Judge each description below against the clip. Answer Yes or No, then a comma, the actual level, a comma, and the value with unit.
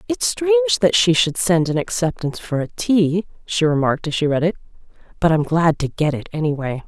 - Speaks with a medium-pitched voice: Yes, medium, 170 Hz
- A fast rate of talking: Yes, fast, 210 wpm